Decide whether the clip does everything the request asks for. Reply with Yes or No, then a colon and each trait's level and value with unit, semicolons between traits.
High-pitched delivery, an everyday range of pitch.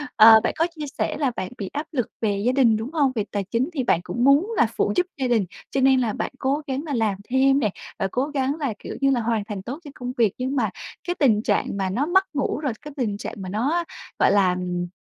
Yes: very high, 250 Hz; average, 4.8 semitones